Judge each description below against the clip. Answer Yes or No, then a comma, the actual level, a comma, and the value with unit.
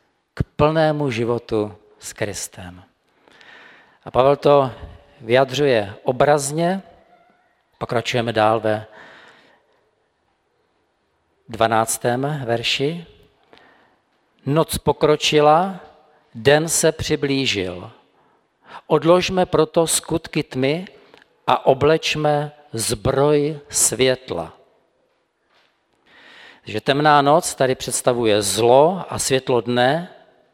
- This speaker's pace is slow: Yes, slow, 70 wpm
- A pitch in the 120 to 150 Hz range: Yes, medium, 140 Hz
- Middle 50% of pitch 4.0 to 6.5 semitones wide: Yes, average, 4.6 semitones